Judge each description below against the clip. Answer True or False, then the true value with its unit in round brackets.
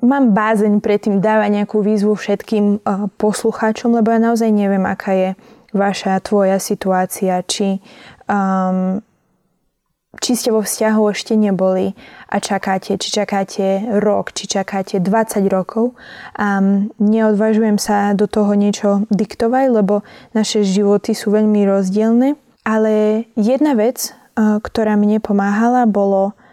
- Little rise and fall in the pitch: True (1.8 semitones)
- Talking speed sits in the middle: False (130 wpm)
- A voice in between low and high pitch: False (210 Hz)